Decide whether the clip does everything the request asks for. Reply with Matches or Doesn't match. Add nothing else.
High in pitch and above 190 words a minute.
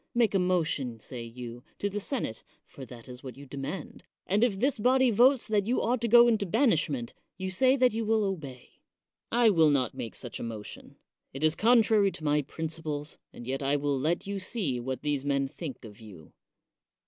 Doesn't match